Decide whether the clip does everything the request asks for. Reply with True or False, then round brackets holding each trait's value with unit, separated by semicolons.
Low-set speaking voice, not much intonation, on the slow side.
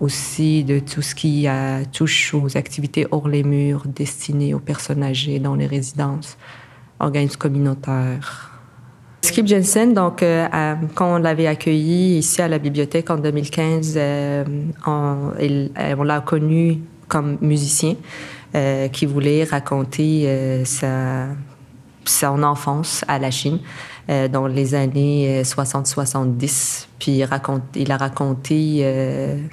False (145 Hz; 2.2 semitones; 135 wpm)